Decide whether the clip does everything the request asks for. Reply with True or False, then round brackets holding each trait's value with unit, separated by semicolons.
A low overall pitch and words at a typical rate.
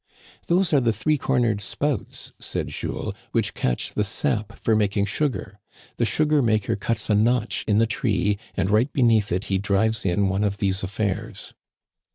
True (110 Hz; 175 wpm)